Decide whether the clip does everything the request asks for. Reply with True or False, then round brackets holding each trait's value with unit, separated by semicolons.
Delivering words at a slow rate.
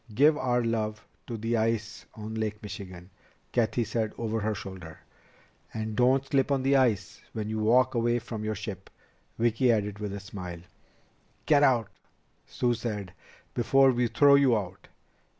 False (160 wpm)